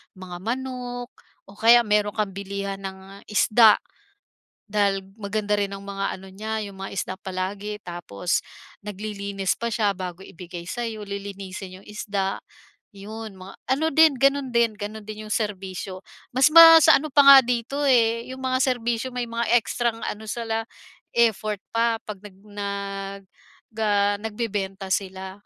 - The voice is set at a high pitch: Yes, high, 210 Hz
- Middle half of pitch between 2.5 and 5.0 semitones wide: Yes, average, 2.9 semitones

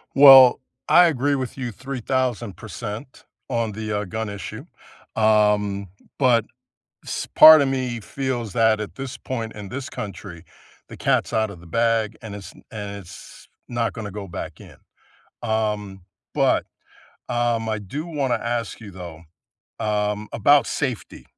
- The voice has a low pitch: Yes, low, 110 Hz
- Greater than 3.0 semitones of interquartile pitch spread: Yes, average, 3.7 semitones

